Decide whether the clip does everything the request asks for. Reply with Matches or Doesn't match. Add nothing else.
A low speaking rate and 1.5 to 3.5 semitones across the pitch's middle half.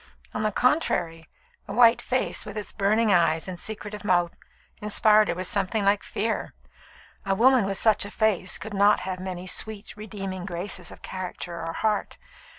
Doesn't match